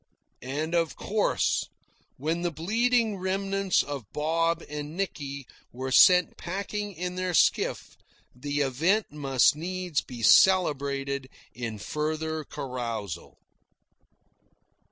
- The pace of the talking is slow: Yes, slow, 105 wpm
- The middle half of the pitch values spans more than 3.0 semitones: Yes, average, 5.0 semitones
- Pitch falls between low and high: Yes, medium, 155 Hz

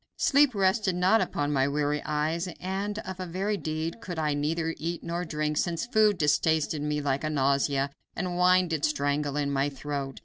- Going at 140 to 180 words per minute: No, average, 190 wpm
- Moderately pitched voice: Yes, medium, 155 Hz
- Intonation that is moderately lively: Yes, average, 3.9 semitones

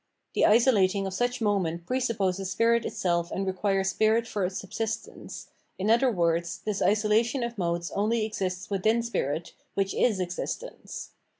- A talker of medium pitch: No, high, 200 Hz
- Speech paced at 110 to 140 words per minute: No, average, 160 wpm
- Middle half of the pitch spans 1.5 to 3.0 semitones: No, average, 3.7 semitones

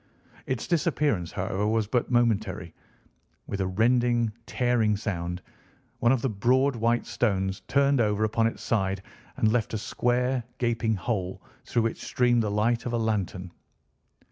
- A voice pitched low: Yes, low, 115 Hz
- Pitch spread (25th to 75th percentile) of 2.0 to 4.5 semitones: Yes, average, 3.3 semitones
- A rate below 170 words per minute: Yes, average, 150 wpm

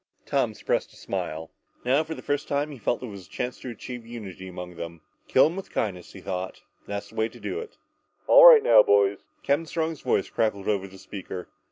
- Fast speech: Yes, fast, 220 wpm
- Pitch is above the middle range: No, low, 115 Hz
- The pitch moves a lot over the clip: Yes, wide, 8.5 semitones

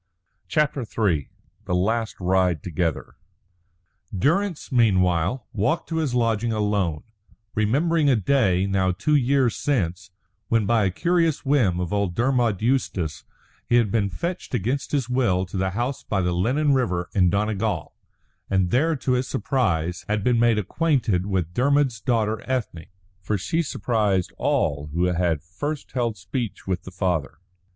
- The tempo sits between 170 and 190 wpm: No, average, 150 wpm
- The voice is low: Yes, low, 105 Hz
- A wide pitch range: Yes, wide, 6.0 semitones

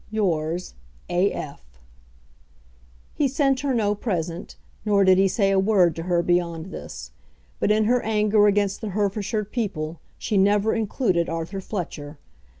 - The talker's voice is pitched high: Yes, high, 195 Hz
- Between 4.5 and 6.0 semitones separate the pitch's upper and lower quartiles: No, average, 3.5 semitones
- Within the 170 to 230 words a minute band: No, average, 150 wpm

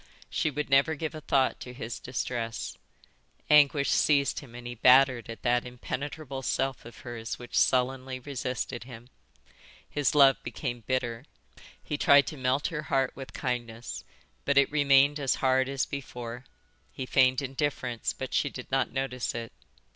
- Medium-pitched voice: No, low, 130 Hz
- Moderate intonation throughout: No, narrow, 2.3 semitones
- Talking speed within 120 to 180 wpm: Yes, average, 160 wpm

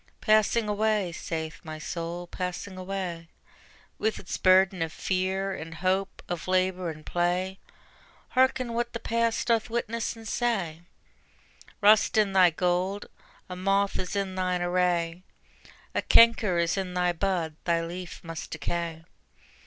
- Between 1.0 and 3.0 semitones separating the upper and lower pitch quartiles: Yes, average, 2.7 semitones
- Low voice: No, medium, 185 Hz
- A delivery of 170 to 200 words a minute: No, average, 140 wpm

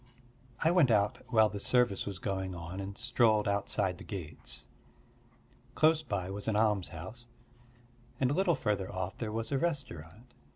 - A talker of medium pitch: No, low, 105 Hz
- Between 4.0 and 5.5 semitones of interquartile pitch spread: Yes, average, 4.5 semitones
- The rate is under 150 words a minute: No, average, 160 wpm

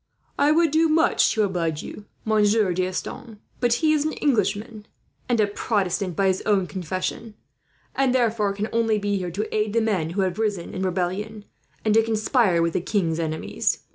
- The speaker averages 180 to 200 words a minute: Yes, average, 185 wpm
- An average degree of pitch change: Yes, average, 3.5 semitones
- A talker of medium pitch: No, high, 210 Hz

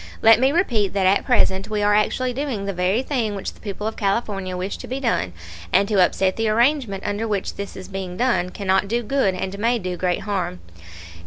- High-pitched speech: Yes, high, 205 Hz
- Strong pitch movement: No, average, 3.5 semitones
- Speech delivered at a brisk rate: Yes, fast, 220 wpm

